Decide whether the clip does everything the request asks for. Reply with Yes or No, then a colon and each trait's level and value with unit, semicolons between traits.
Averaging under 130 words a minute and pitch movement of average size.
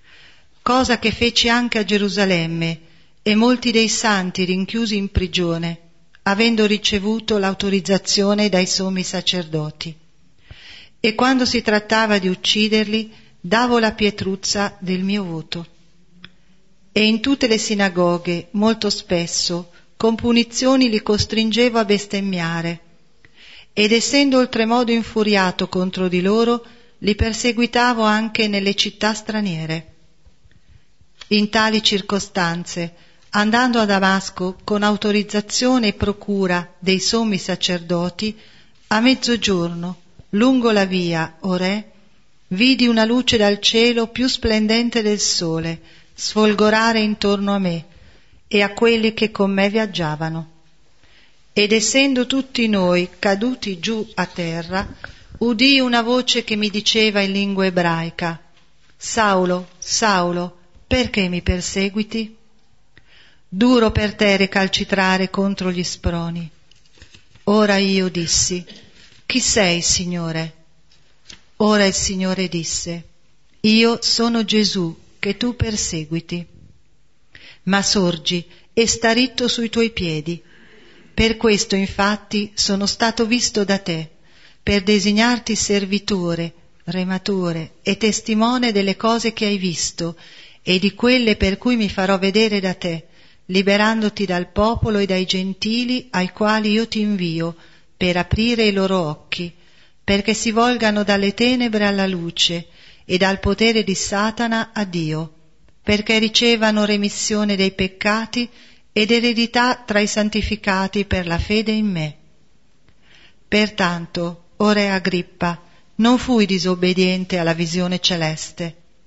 Yes: average, 120 wpm; average, 3.7 semitones